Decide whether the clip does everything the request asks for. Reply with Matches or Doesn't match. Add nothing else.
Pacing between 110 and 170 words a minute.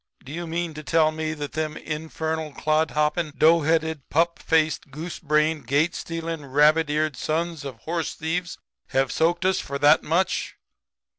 Matches